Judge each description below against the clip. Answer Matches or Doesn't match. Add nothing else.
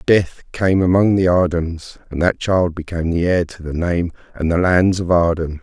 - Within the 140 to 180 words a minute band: Doesn't match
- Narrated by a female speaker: Doesn't match